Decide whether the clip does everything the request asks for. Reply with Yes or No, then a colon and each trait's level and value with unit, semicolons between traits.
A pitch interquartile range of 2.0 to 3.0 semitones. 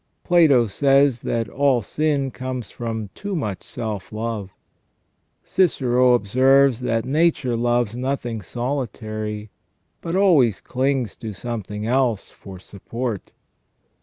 No: average, 4.0 semitones